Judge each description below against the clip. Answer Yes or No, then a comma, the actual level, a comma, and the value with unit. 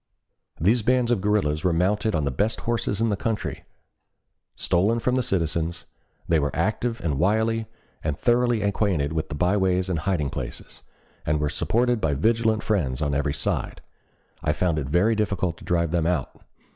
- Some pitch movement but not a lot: No, wide, 6.0 semitones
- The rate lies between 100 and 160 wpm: No, average, 175 wpm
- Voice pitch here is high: No, very low, 95 Hz